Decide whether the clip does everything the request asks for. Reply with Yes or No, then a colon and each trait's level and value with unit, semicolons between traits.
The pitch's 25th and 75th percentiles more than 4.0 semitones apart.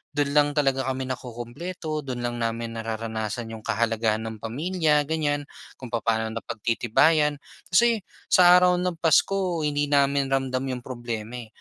Yes: average, 4.8 semitones